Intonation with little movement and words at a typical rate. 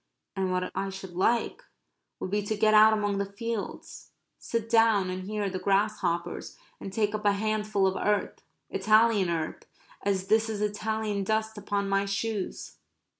Yes: narrow, 1.9 semitones; average, 165 wpm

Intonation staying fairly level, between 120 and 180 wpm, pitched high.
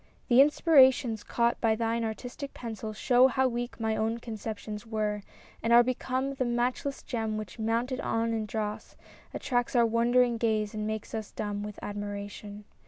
Yes: narrow, 2.2 semitones; average, 170 wpm; high, 230 Hz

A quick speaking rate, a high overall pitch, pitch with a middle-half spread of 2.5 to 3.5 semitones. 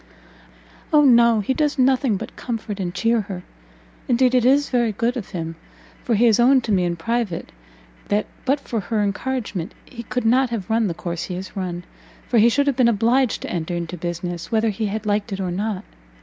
No: fast, 215 wpm; high, 220 Hz; average, 4.7 semitones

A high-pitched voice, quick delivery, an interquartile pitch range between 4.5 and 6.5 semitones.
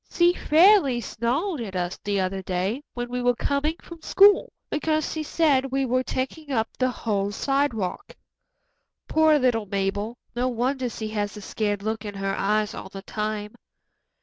No: high, 240 Hz; average, 170 wpm; wide, 5.4 semitones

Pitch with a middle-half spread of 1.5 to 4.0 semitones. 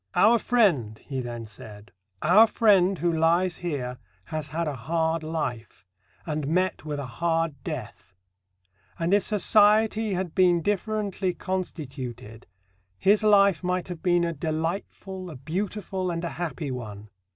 No: average, 4.8 semitones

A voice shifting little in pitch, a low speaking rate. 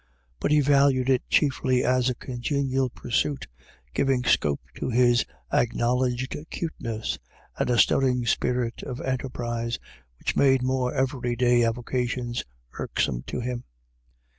Yes: narrow, 1.6 semitones; slow, 120 wpm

